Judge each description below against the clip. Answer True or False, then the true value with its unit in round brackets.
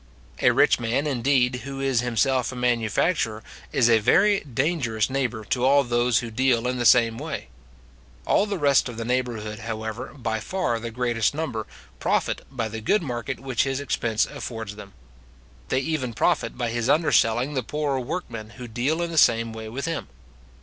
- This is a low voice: True (125 Hz)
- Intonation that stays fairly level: False (3.2 semitones)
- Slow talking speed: False (180 wpm)